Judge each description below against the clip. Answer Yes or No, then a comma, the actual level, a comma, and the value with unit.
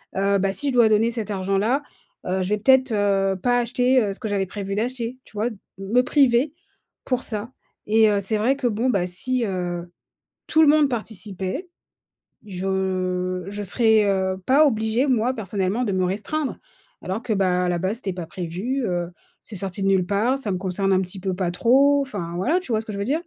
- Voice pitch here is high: Yes, high, 205 Hz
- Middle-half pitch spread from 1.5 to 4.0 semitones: No, average, 4.4 semitones